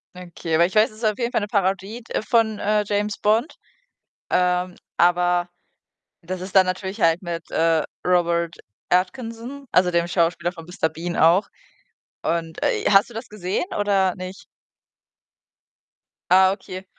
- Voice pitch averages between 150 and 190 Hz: Yes, medium, 185 Hz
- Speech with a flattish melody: No, average, 3.2 semitones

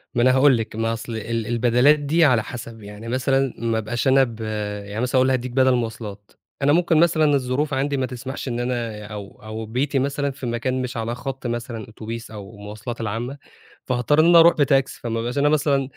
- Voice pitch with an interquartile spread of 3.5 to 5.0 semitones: No, average, 3.1 semitones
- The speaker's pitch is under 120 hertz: No, low, 125 Hz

